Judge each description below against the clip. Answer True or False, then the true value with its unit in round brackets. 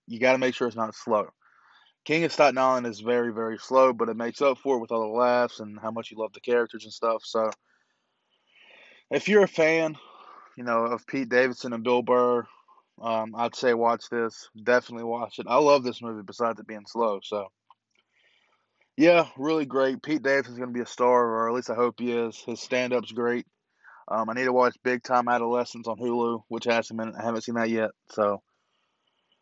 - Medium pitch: False (120 Hz)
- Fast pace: True (210 wpm)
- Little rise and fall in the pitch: True (1.8 semitones)